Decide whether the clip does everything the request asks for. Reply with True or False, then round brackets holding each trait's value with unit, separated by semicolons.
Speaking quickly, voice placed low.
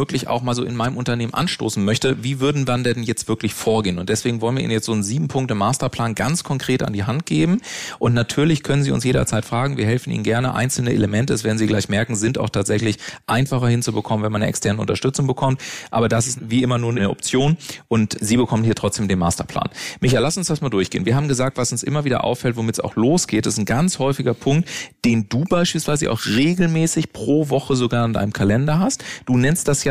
True (230 wpm; 120 Hz)